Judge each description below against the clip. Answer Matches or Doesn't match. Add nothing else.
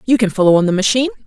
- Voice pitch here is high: Matches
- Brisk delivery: Matches